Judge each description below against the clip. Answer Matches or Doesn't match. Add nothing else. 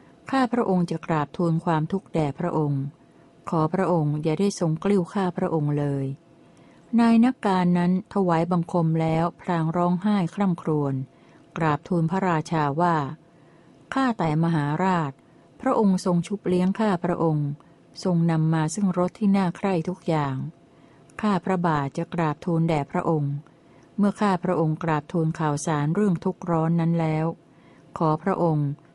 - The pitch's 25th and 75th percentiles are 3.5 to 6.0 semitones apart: Doesn't match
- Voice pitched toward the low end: Doesn't match